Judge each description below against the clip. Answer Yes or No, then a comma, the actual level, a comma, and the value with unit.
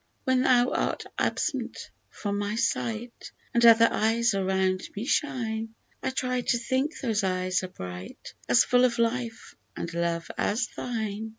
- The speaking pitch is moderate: No, high, 225 Hz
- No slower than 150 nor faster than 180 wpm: Yes, average, 155 wpm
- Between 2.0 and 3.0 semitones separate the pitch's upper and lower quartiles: No, average, 4.2 semitones